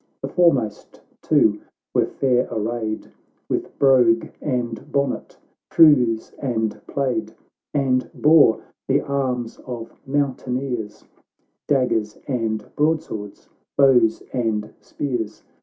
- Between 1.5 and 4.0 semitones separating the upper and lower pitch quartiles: Yes, average, 3.5 semitones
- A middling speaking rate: No, slow, 95 wpm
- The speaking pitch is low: Yes, low, 125 Hz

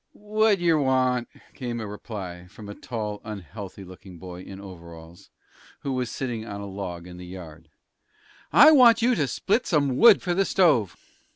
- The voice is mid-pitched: No, low, 110 Hz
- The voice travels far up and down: Yes, wide, 8.5 semitones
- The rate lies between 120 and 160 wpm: No, average, 180 wpm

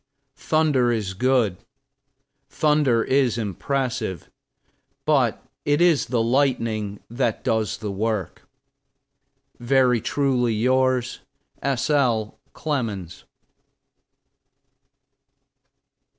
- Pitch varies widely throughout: No, average, 3.7 semitones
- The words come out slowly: Yes, slow, 80 wpm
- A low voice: Yes, low, 120 Hz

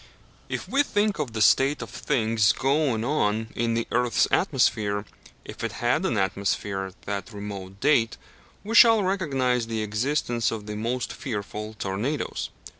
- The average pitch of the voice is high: No, low, 115 Hz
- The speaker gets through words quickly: No, average, 155 wpm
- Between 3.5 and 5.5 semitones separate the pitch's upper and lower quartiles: Yes, average, 4.8 semitones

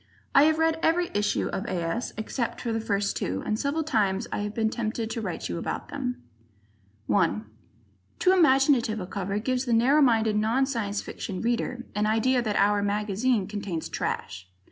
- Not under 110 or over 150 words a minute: No, average, 185 wpm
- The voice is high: Yes, high, 220 Hz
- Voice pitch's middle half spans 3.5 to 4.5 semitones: Yes, average, 4.1 semitones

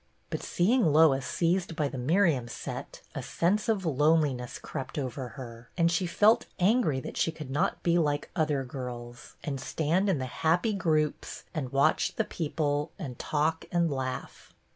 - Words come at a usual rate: Yes, average, 170 wpm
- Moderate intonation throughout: Yes, average, 4.3 semitones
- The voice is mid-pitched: Yes, medium, 155 Hz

